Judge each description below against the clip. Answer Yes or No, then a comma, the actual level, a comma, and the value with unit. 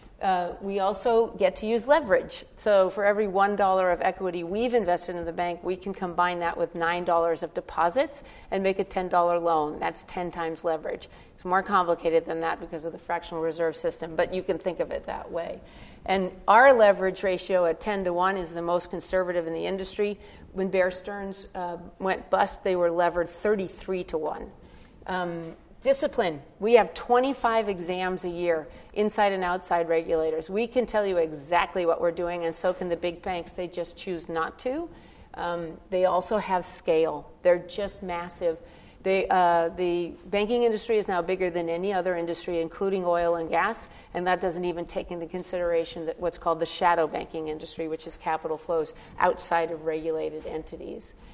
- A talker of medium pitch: Yes, medium, 180 Hz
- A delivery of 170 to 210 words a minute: Yes, average, 185 wpm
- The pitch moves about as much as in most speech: No, narrow, 2.3 semitones